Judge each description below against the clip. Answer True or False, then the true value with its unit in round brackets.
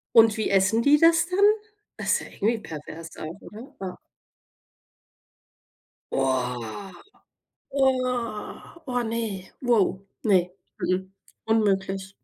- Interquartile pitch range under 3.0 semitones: False (4.3 semitones)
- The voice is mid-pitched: False (205 Hz)